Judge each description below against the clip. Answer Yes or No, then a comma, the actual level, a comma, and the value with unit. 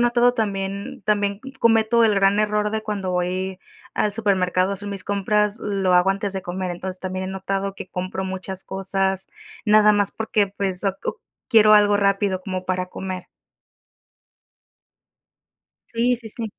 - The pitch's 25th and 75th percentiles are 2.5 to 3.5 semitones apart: No, narrow, 1.9 semitones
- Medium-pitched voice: No, high, 195 Hz